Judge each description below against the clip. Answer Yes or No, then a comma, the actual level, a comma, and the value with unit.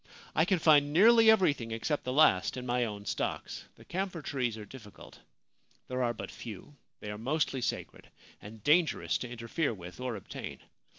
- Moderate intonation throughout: No, wide, 5.7 semitones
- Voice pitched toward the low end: Yes, low, 125 Hz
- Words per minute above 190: No, average, 175 wpm